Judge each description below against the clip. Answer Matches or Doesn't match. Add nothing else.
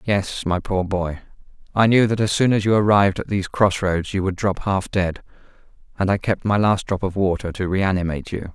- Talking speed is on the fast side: Matches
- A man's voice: Matches